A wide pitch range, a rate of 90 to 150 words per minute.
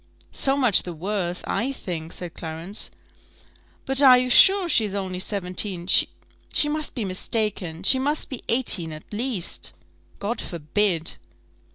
Yes: wide, 6.3 semitones; average, 140 wpm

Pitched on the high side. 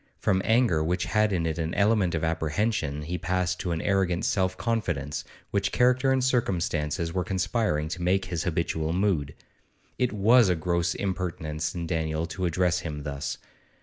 No: very low, 90 Hz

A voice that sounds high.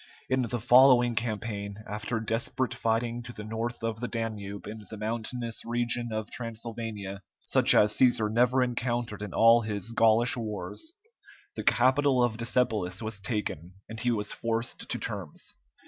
No: low, 115 Hz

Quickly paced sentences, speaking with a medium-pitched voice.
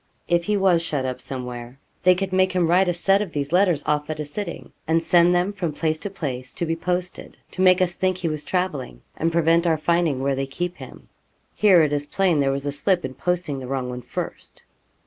Yes: fast, 235 wpm; medium, 165 Hz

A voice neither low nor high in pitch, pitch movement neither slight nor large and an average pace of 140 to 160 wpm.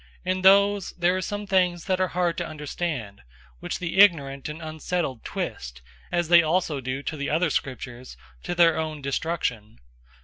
No: medium, 165 Hz; average, 4.7 semitones; average, 170 wpm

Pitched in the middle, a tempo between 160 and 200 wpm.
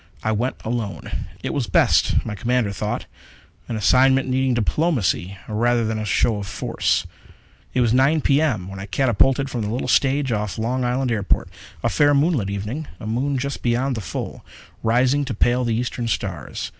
No: low, 120 Hz; average, 180 wpm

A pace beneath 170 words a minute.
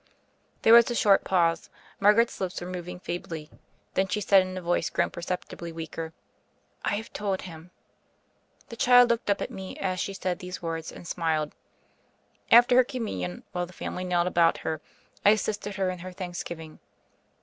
No: average, 175 wpm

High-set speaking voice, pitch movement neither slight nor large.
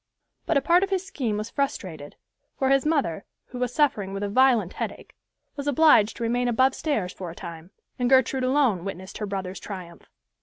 No: high, 240 Hz; wide, 6.0 semitones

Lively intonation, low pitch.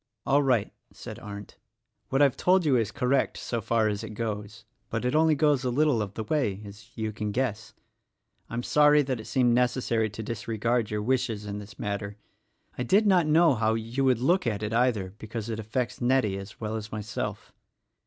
No: average, 3.7 semitones; low, 115 Hz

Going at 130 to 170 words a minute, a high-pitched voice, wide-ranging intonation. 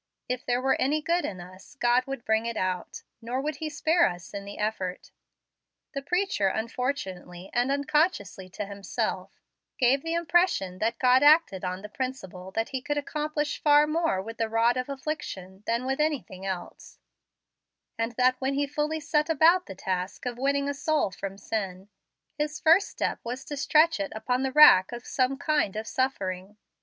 No: average, 180 wpm; very high, 255 Hz; wide, 6.8 semitones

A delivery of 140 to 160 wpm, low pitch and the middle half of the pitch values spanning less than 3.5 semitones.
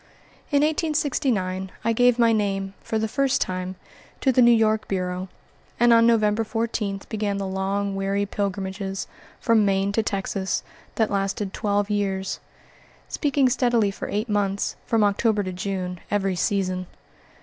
No: average, 150 wpm; high, 205 Hz; average, 2.9 semitones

